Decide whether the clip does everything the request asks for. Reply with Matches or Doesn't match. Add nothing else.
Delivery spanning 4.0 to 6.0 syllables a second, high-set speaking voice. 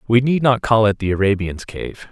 Doesn't match